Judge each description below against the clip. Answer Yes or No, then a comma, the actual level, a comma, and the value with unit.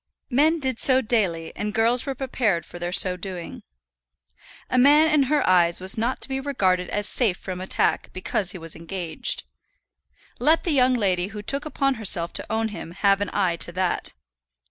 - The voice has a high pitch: Yes, high, 210 Hz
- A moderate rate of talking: Yes, average, 190 wpm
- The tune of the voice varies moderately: No, wide, 6.3 semitones